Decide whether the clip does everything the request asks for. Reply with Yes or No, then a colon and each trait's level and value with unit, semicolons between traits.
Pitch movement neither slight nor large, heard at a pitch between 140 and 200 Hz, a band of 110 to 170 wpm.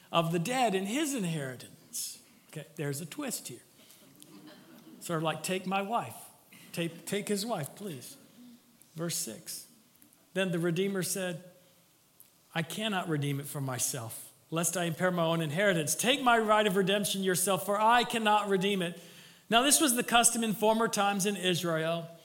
Yes: average, 4.1 semitones; medium, 185 Hz; average, 165 wpm